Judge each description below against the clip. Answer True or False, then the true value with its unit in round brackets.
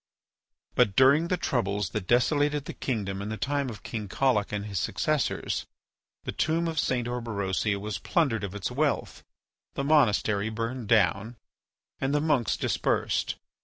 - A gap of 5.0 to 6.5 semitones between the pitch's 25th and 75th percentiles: True (5.4 semitones)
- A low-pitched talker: True (115 Hz)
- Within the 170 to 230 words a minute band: False (155 wpm)